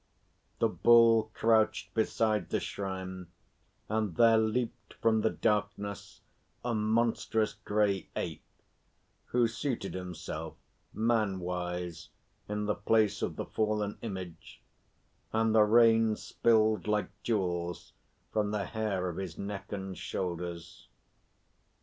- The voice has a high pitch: No, low, 105 Hz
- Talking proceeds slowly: Yes, slow, 115 wpm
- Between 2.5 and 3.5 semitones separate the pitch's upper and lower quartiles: Yes, average, 3.0 semitones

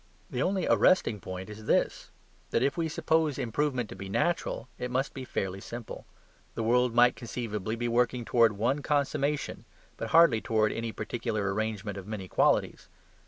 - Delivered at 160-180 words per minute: Yes, average, 165 wpm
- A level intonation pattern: No, average, 4.2 semitones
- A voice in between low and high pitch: No, low, 120 Hz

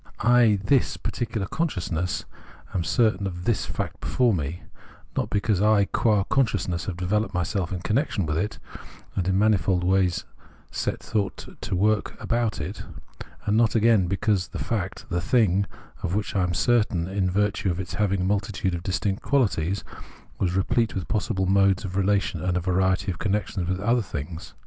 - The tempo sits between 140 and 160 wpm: No, average, 180 wpm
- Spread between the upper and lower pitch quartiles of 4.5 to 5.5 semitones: No, average, 3.0 semitones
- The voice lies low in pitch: Yes, very low, 95 Hz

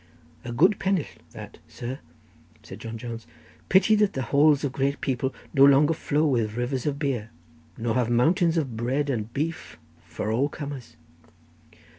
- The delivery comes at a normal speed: Yes, average, 165 wpm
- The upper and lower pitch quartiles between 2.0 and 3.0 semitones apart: No, average, 3.9 semitones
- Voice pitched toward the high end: No, low, 135 Hz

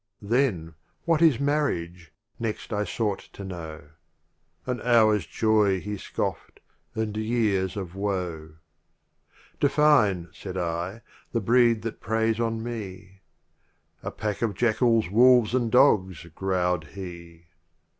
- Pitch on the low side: Yes, low, 105 Hz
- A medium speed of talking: No, slow, 130 wpm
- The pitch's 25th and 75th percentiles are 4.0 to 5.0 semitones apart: Yes, average, 4.3 semitones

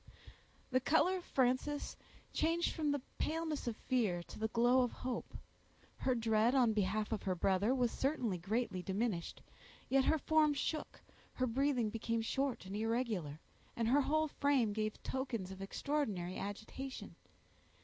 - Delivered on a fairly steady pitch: No, average, 4.5 semitones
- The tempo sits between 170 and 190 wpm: No, average, 150 wpm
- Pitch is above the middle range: Yes, high, 240 Hz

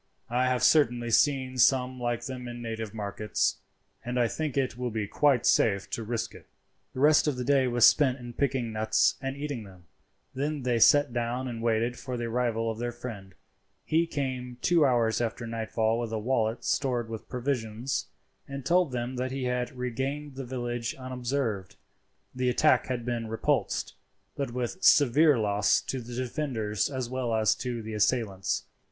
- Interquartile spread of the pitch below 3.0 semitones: Yes, narrow, 2.5 semitones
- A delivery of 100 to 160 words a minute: No, average, 180 wpm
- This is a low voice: Yes, low, 125 Hz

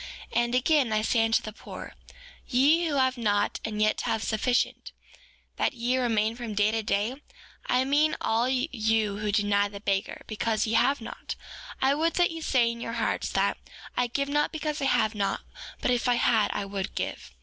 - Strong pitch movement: No, average, 3.6 semitones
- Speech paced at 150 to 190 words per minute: No, average, 200 wpm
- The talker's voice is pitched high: Yes, high, 235 Hz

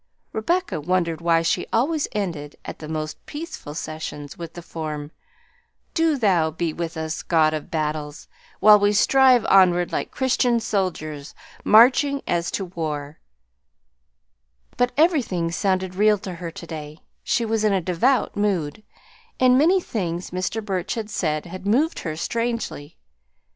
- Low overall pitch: No, medium, 185 Hz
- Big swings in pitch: Yes, wide, 6.1 semitones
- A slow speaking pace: No, average, 150 wpm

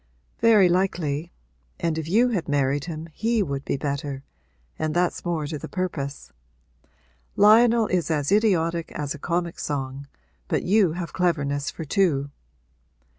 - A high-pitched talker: No, medium, 165 Hz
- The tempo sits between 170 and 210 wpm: No, average, 145 wpm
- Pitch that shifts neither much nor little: Yes, average, 4.5 semitones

